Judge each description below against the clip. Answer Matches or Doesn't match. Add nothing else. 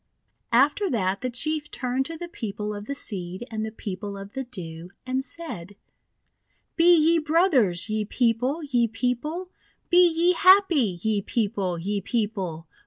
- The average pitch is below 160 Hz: Doesn't match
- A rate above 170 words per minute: Doesn't match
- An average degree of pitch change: Doesn't match